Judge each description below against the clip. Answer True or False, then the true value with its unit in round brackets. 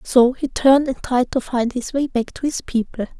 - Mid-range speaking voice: False (255 Hz)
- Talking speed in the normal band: False (245 wpm)